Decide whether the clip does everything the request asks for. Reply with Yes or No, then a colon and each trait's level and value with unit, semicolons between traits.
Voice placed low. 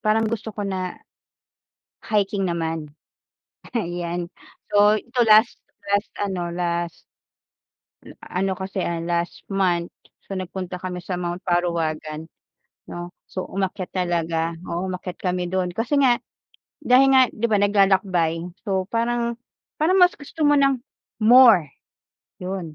No: medium, 185 Hz